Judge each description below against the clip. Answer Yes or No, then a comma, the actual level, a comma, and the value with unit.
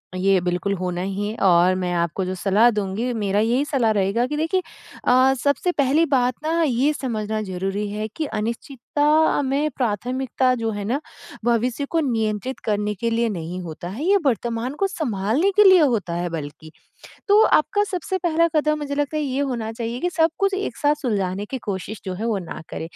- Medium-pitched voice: No, high, 235 Hz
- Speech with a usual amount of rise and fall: No, wide, 6.6 semitones